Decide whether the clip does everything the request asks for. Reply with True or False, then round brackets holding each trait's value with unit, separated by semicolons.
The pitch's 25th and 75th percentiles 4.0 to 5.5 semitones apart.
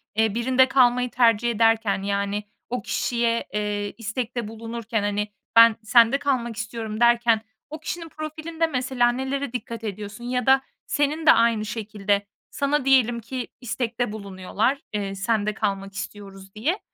False (3.3 semitones)